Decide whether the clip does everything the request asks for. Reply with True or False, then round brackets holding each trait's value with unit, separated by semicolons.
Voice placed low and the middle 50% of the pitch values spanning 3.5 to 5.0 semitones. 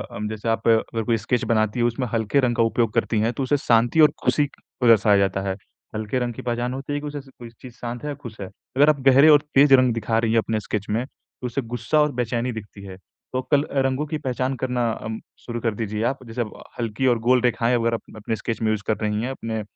False (120 Hz; 2.8 semitones)